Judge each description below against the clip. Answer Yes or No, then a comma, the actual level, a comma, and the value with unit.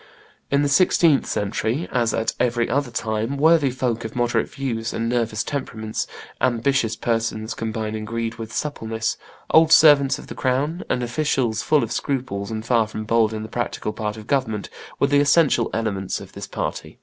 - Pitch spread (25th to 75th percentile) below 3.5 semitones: No, average, 3.8 semitones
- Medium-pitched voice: No, low, 115 Hz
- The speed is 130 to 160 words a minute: No, average, 175 wpm